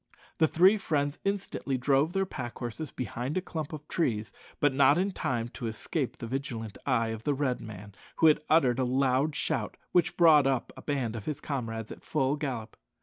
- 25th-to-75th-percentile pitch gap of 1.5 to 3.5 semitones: No, average, 4.4 semitones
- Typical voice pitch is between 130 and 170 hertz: Yes, low, 135 Hz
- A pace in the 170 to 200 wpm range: Yes, average, 195 wpm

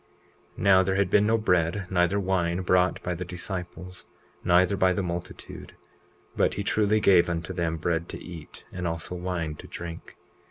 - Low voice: Yes, very low, 90 Hz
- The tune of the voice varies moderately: No, narrow, 1.8 semitones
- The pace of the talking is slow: No, average, 185 wpm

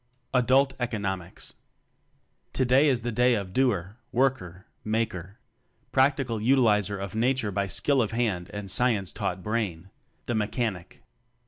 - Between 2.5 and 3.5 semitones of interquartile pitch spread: No, average, 4.3 semitones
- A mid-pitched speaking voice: No, low, 110 Hz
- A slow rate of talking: Yes, slow, 130 wpm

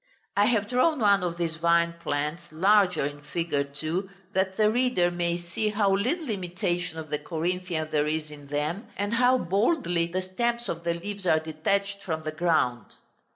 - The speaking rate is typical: Yes, average, 180 wpm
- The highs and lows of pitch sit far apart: No, average, 4.2 semitones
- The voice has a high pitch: No, medium, 175 Hz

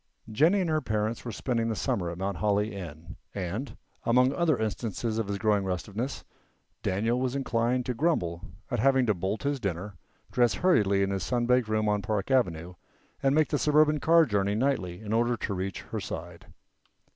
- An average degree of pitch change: Yes, average, 4.6 semitones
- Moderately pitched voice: No, low, 110 Hz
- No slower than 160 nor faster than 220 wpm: Yes, average, 190 wpm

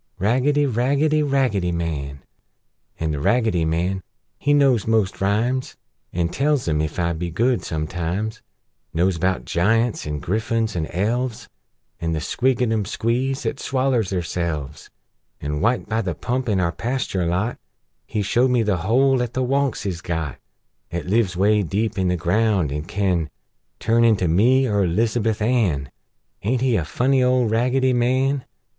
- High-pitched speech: No, low, 110 Hz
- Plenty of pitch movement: Yes, wide, 6.3 semitones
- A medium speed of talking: Yes, average, 155 wpm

